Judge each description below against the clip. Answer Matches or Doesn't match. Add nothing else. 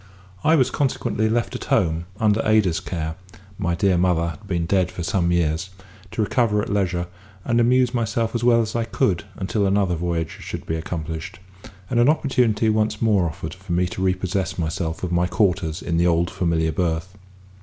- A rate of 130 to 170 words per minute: Doesn't match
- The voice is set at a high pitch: Doesn't match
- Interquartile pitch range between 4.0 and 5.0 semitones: Matches